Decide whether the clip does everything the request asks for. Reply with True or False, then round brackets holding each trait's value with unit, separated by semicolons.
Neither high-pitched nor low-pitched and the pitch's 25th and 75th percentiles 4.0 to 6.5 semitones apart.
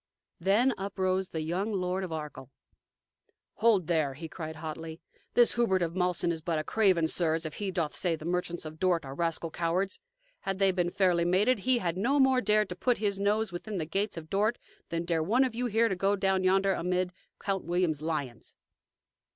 False (180 Hz; 3.4 semitones)